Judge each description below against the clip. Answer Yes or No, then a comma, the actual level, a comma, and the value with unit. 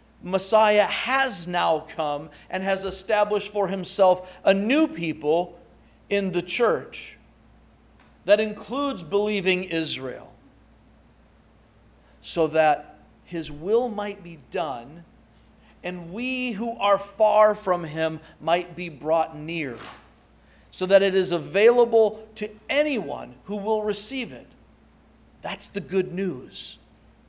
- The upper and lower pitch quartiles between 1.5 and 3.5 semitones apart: No, average, 4.1 semitones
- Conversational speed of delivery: No, slow, 115 wpm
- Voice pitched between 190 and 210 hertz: Yes, high, 195 Hz